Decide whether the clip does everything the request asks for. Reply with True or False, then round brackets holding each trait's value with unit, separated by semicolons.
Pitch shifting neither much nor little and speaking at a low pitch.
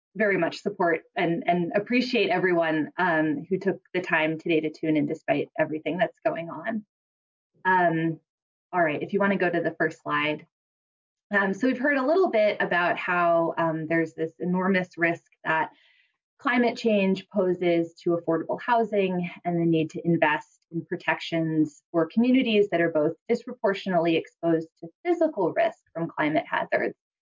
False (4.1 semitones; 170 Hz)